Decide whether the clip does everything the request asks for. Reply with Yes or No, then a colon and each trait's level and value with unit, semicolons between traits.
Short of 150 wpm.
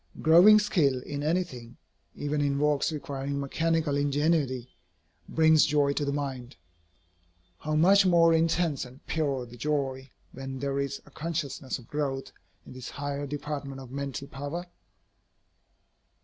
Yes: slow, 135 wpm